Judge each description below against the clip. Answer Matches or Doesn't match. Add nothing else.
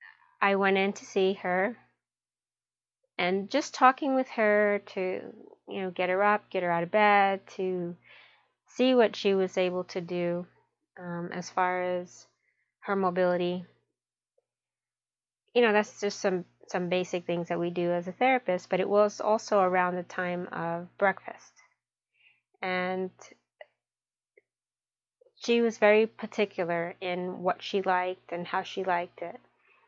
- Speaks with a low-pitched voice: Doesn't match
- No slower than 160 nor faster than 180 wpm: Doesn't match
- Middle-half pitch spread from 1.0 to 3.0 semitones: Matches